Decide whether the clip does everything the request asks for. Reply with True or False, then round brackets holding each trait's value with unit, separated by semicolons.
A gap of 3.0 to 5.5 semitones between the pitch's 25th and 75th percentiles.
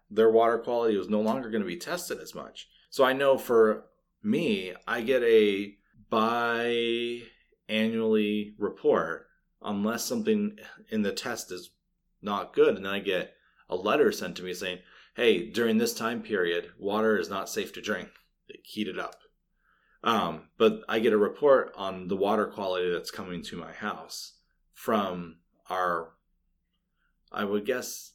False (2.6 semitones)